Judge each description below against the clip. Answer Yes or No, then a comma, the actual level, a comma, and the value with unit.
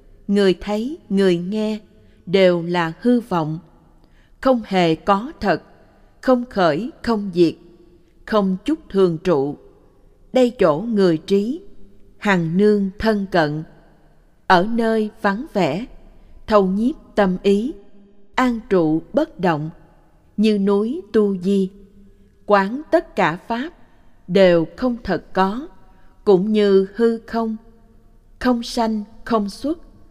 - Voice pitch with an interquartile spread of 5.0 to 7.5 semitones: No, average, 4.0 semitones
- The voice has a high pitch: Yes, high, 200 Hz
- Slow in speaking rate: Yes, slow, 120 wpm